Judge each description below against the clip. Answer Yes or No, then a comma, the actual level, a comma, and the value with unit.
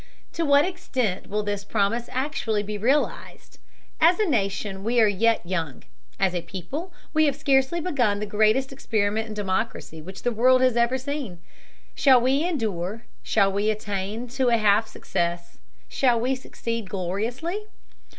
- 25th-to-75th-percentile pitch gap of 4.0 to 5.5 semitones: Yes, average, 4.8 semitones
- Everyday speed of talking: Yes, average, 160 wpm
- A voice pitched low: No, high, 225 Hz